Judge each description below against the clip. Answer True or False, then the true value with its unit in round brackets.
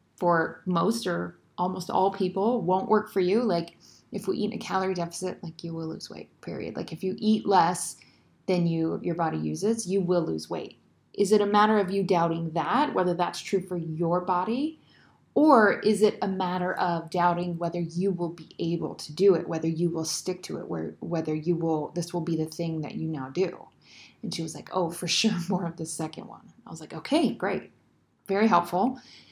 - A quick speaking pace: True (215 wpm)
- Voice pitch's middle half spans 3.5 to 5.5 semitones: False (2.8 semitones)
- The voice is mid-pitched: True (175 Hz)